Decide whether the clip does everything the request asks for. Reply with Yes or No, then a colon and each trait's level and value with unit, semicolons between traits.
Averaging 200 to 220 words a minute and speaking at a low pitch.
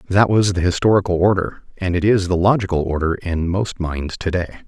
Yes: fast, 205 wpm; very low, 90 Hz